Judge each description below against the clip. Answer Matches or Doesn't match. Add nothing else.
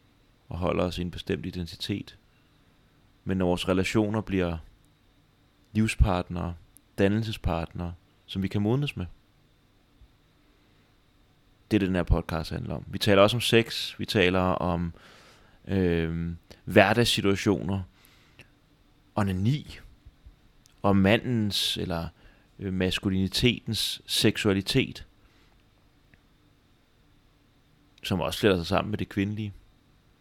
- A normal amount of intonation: Matches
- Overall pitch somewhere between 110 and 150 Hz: Doesn't match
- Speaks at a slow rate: Matches